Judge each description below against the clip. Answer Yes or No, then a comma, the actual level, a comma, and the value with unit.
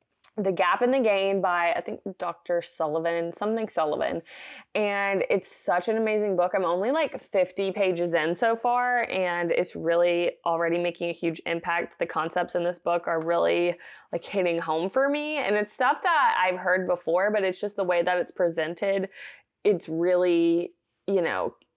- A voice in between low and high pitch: Yes, medium, 180 Hz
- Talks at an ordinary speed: Yes, average, 180 wpm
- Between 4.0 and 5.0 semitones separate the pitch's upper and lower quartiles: No, average, 3.2 semitones